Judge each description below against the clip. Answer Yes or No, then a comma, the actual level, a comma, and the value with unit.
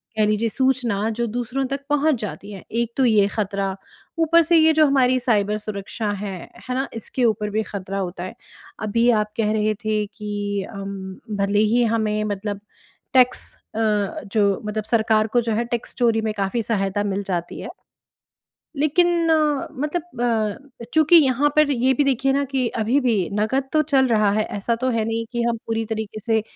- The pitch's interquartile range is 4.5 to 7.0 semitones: No, average, 3.9 semitones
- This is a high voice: Yes, high, 225 Hz